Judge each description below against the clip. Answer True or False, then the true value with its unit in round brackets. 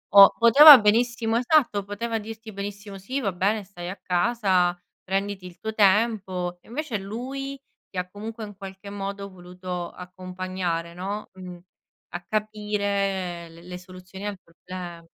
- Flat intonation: False (3.1 semitones)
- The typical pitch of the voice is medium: False (200 Hz)